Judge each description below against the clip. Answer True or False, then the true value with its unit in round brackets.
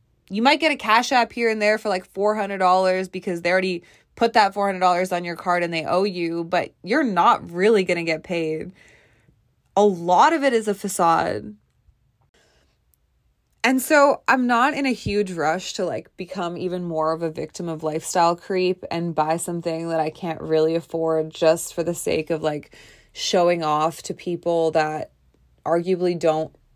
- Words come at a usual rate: True (180 wpm)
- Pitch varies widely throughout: False (3.4 semitones)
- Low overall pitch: False (175 Hz)